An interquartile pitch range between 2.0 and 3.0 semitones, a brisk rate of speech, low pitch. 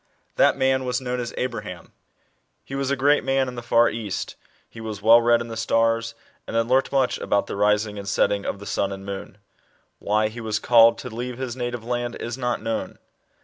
Yes: narrow, 2.4 semitones; fast, 215 wpm; low, 115 Hz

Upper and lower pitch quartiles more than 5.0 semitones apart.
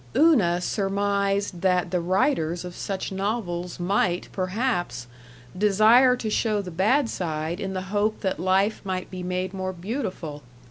No: average, 2.8 semitones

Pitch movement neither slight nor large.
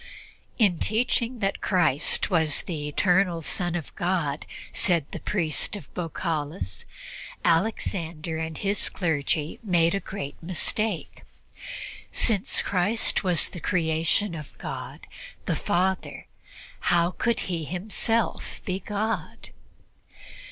Yes: average, 3.7 semitones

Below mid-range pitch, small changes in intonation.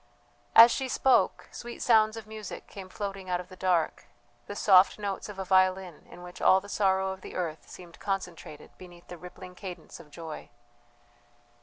No: high, 190 Hz; narrow, 2.3 semitones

